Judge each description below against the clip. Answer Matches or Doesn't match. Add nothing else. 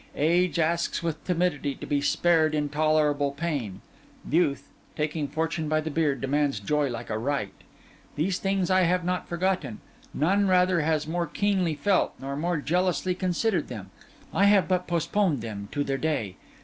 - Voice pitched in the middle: Matches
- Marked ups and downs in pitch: Doesn't match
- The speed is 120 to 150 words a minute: Doesn't match